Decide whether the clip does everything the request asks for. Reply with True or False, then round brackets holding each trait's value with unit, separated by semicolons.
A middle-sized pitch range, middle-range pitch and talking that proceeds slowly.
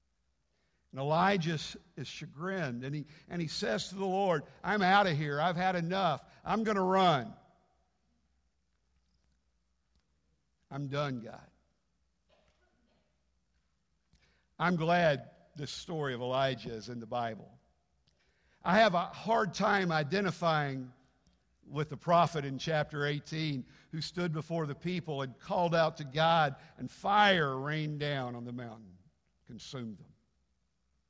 False (7.4 semitones; 145 Hz; 130 wpm)